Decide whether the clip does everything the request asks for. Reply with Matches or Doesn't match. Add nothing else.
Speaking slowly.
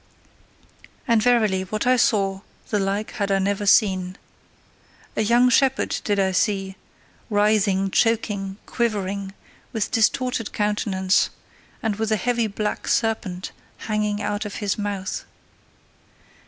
Matches